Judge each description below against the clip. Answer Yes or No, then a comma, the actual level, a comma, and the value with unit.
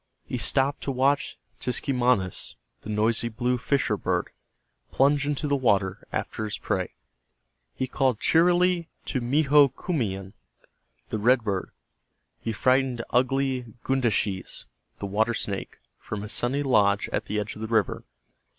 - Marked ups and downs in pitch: No, average, 4.3 semitones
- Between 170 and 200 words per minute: No, slow, 135 wpm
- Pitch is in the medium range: No, low, 125 Hz